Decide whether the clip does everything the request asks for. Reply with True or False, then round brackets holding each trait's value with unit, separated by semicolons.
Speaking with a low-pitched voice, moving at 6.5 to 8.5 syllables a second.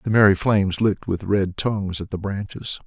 False (100 Hz; 5.5 syllables/s)